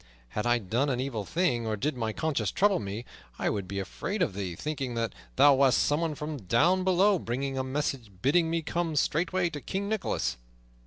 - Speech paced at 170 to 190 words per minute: No, average, 200 wpm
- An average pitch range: No, wide, 6.3 semitones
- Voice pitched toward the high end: No, medium, 140 Hz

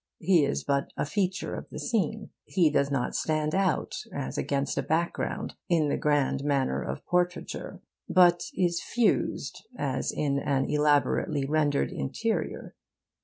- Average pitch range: Yes, average, 3.9 semitones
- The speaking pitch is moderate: Yes, medium, 150 Hz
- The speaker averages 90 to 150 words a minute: Yes, average, 145 wpm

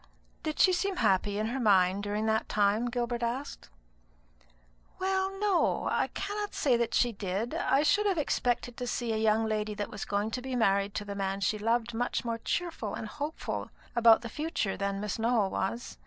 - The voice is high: Yes, high, 230 Hz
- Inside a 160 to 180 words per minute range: No, average, 195 wpm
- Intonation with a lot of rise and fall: No, average, 4.3 semitones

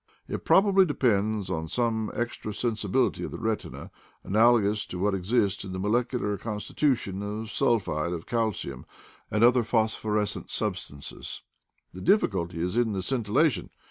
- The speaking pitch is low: Yes, low, 105 Hz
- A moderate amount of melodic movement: Yes, average, 3.6 semitones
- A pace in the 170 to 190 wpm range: No, average, 155 wpm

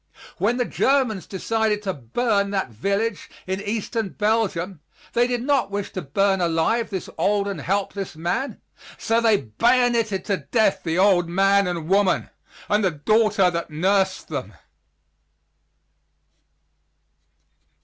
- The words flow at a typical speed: No, slow, 130 wpm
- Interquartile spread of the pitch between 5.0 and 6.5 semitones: No, average, 3.7 semitones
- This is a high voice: Yes, high, 200 Hz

